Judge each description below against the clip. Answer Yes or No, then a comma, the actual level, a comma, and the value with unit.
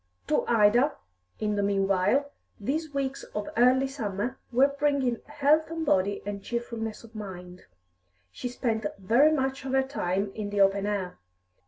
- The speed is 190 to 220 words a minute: No, average, 155 wpm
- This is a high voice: Yes, high, 230 Hz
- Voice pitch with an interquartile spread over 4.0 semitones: Yes, average, 5.0 semitones